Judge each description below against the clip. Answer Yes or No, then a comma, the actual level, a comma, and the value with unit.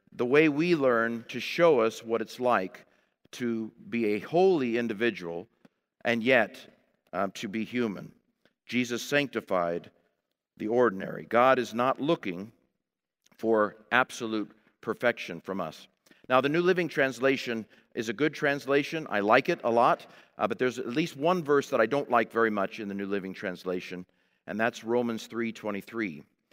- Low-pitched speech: Yes, low, 120 Hz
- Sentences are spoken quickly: No, average, 160 wpm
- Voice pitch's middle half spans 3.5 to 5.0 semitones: Yes, average, 4.1 semitones